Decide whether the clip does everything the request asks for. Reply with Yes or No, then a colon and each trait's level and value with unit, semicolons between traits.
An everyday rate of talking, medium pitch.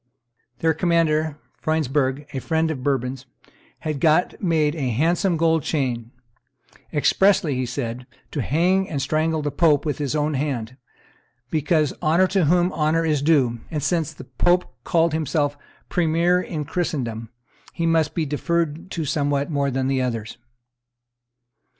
Yes: average, 145 wpm; medium, 155 Hz